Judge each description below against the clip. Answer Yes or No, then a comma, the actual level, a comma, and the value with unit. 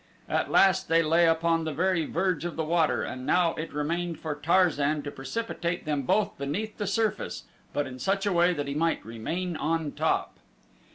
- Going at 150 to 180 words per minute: No, average, 190 wpm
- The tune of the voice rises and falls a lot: No, average, 3.4 semitones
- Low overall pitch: No, medium, 165 Hz